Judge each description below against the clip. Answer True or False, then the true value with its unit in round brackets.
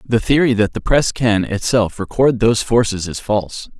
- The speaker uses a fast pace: False (190 wpm)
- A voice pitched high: False (110 Hz)